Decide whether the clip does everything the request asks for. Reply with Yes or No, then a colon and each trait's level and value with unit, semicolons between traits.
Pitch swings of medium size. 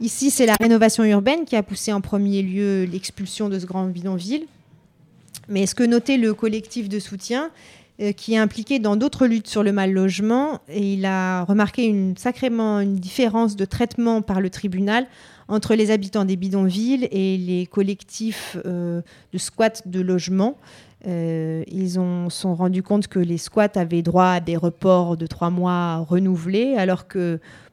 Yes: average, 3.3 semitones